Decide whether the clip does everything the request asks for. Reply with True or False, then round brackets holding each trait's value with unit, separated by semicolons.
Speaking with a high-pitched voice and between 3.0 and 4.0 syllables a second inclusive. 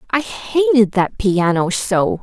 True (220 Hz; 3.5 syllables/s)